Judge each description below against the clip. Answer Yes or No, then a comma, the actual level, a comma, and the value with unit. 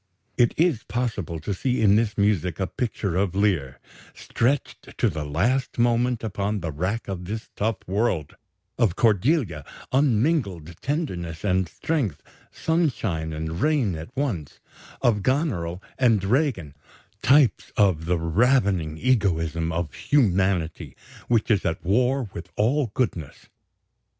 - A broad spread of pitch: Yes, wide, 6.5 semitones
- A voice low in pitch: Yes, low, 100 Hz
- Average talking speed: No, slow, 130 wpm